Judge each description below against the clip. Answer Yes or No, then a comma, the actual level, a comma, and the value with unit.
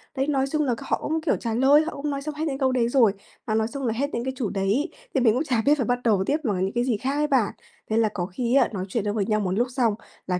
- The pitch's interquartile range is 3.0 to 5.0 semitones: Yes, average, 4.3 semitones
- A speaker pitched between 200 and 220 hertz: No, high, 245 Hz